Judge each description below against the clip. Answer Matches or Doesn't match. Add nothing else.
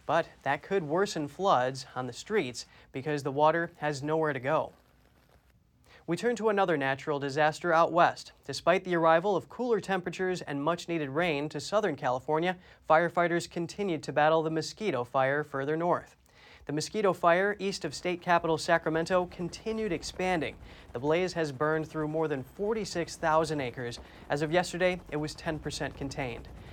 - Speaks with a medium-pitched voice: Matches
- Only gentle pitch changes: Doesn't match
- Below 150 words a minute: Doesn't match